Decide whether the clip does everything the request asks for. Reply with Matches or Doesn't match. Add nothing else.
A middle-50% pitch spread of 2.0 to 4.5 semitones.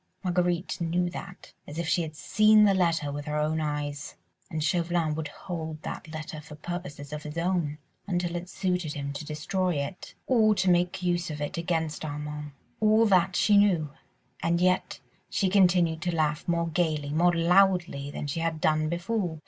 Matches